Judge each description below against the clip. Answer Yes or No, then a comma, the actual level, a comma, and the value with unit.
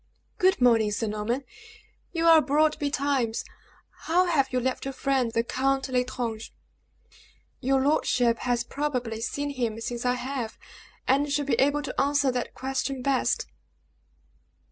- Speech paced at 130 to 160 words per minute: Yes, average, 145 wpm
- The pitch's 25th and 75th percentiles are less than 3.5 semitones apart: Yes, average, 2.9 semitones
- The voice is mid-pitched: No, very high, 260 Hz